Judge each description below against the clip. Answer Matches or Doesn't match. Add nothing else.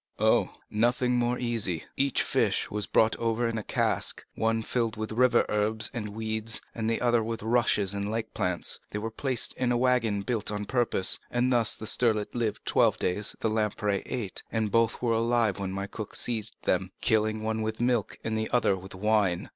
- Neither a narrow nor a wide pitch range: Doesn't match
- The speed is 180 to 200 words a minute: Matches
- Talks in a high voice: Doesn't match